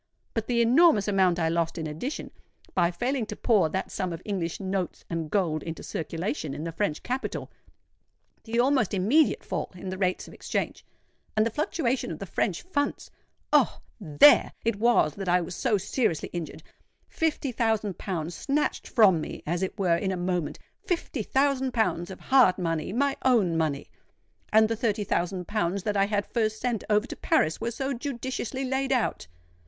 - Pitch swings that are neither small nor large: No, wide, 5.8 semitones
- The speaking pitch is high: Yes, high, 205 Hz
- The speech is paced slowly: No, average, 175 wpm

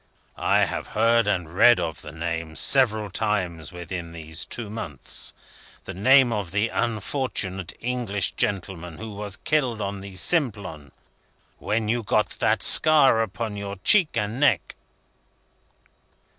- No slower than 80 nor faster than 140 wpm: Yes, slow, 135 wpm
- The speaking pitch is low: Yes, low, 105 Hz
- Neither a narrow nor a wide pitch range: Yes, average, 4.5 semitones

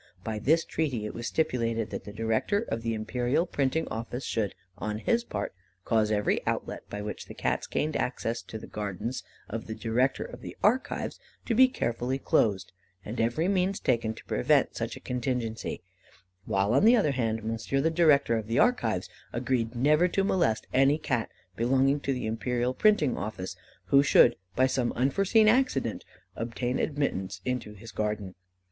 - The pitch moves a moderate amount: Yes, average, 4.5 semitones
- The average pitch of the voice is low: Yes, low, 120 Hz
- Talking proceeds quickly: No, average, 175 wpm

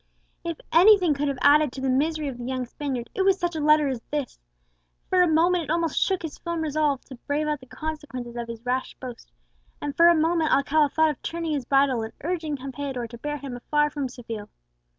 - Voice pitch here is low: No, very high, 295 Hz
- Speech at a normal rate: No, fast, 220 wpm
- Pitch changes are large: No, average, 3.6 semitones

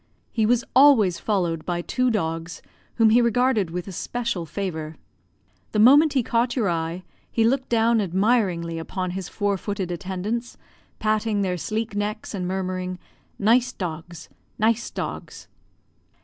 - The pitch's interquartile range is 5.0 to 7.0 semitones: No, average, 4.5 semitones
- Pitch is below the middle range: No, high, 205 Hz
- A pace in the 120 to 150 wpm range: Yes, average, 140 wpm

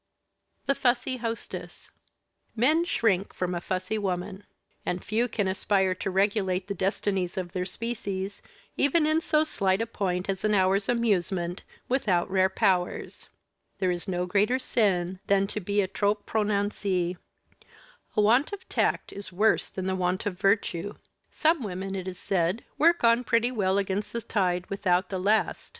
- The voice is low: No, high, 195 Hz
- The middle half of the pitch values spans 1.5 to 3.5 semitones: Yes, average, 3.2 semitones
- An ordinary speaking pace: Yes, average, 160 wpm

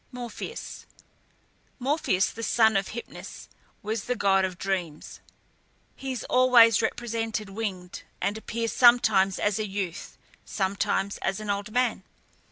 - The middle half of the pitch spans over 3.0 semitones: Yes, average, 3.4 semitones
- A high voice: Yes, high, 215 Hz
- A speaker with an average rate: No, slow, 130 wpm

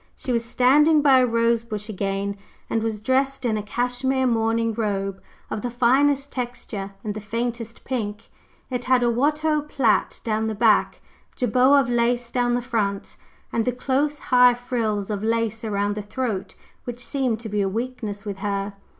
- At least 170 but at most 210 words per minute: Yes, average, 175 wpm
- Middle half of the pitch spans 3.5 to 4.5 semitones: No, average, 3.1 semitones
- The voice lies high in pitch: Yes, high, 235 Hz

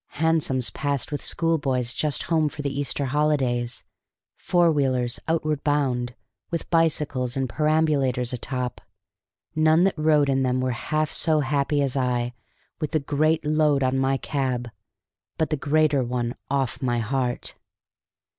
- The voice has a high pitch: No, medium, 140 Hz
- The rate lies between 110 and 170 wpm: Yes, average, 145 wpm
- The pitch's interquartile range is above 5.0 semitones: No, average, 3.3 semitones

